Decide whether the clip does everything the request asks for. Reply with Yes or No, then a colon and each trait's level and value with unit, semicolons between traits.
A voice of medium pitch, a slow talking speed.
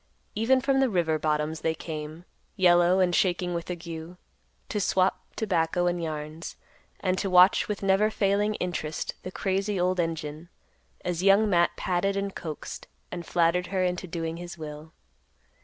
No: medium, 175 Hz; average, 155 wpm